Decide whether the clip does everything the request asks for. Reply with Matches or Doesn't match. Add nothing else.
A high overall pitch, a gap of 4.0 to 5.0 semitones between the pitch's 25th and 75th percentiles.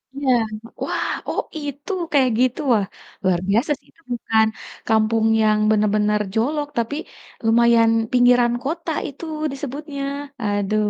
Matches